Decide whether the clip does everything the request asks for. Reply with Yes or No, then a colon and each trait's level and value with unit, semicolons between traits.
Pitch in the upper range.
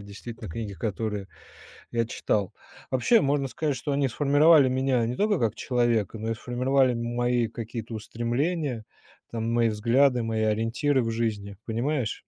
No: low, 120 Hz